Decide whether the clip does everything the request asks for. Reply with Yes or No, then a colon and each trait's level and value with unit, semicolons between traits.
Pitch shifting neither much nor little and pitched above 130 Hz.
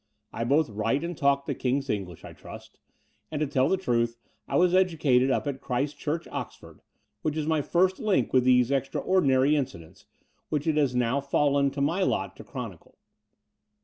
Yes: average, 3.6 semitones; medium, 140 Hz